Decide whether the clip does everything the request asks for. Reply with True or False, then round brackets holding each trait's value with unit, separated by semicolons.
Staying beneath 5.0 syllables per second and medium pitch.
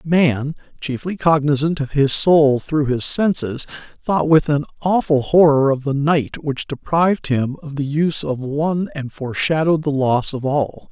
True (4.5 syllables/s; 145 Hz)